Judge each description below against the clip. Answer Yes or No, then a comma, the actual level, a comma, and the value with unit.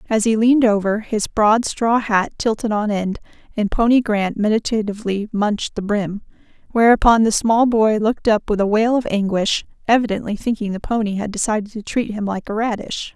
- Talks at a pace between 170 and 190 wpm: Yes, average, 185 wpm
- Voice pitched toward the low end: No, high, 215 Hz